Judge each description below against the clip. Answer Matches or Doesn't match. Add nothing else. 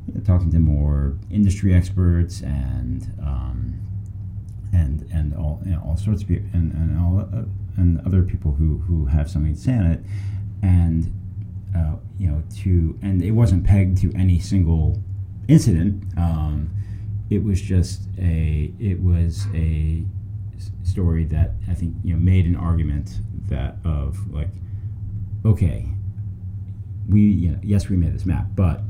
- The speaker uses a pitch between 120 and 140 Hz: Doesn't match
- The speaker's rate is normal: Matches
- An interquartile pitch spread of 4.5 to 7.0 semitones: Doesn't match